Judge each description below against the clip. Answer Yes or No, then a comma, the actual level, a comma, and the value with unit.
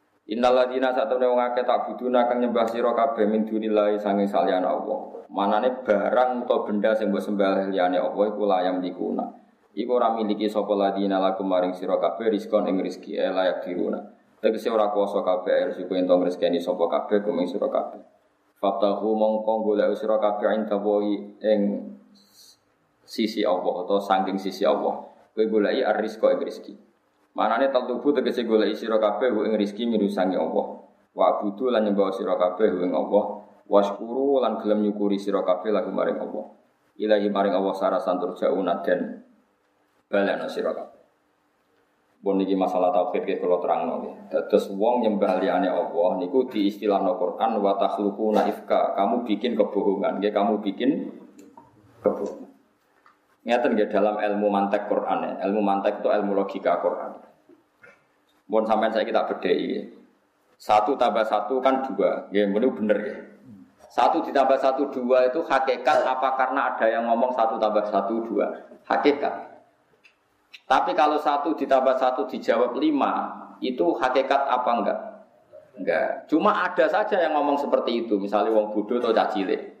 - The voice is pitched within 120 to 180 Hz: No, low, 105 Hz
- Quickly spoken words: Yes, fast, 150 wpm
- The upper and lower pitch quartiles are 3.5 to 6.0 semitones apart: Yes, average, 3.9 semitones